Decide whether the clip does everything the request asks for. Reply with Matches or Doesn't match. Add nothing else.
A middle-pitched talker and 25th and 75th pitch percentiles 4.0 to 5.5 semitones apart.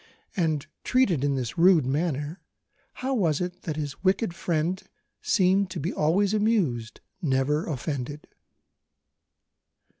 Matches